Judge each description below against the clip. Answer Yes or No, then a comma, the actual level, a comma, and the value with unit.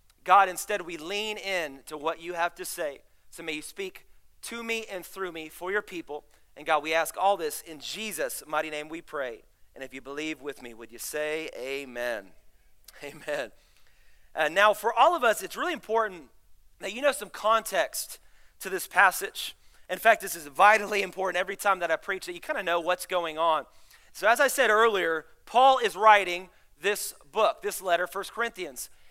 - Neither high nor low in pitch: Yes, medium, 180 Hz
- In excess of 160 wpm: Yes, average, 200 wpm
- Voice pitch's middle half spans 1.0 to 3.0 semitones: No, wide, 5.6 semitones